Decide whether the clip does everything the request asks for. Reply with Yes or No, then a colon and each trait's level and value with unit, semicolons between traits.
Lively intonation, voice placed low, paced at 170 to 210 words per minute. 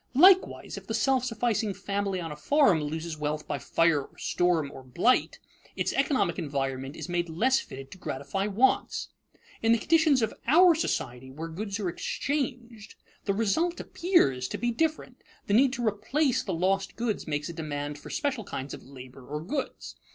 No: wide, 8.9 semitones; high, 195 Hz; average, 180 wpm